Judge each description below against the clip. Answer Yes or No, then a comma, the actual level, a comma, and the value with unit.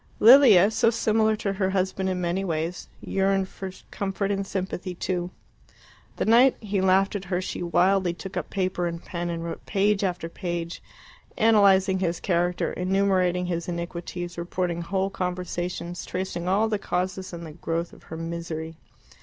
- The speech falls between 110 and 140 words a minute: No, average, 160 wpm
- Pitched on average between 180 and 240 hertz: Yes, medium, 185 Hz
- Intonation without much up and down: Yes, narrow, 2.1 semitones